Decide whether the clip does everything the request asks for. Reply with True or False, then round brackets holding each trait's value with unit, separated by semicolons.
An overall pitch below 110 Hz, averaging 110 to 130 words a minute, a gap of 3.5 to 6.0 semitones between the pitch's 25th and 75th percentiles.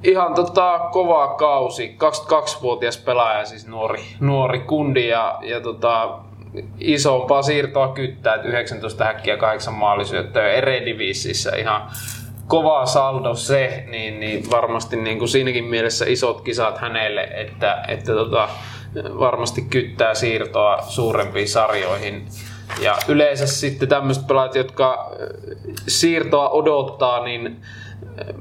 False (120 Hz; 115 wpm; 4.0 semitones)